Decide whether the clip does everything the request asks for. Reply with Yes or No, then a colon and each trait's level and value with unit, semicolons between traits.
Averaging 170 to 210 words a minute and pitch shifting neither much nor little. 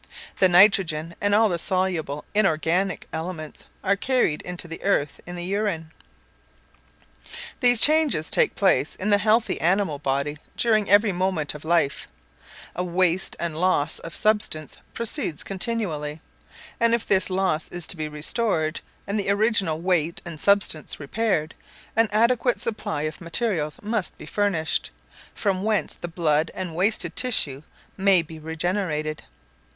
No: average, 145 wpm; average, 4.6 semitones